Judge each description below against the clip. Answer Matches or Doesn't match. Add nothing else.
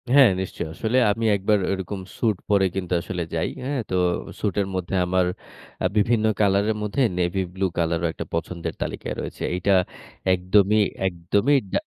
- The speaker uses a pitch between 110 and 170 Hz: Doesn't match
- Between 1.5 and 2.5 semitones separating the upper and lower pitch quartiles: Doesn't match